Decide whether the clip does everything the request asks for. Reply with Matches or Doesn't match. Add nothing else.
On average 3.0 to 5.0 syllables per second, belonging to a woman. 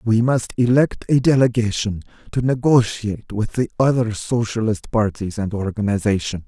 Doesn't match